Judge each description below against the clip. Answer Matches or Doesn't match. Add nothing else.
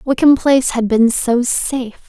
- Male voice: Doesn't match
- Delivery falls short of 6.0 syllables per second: Matches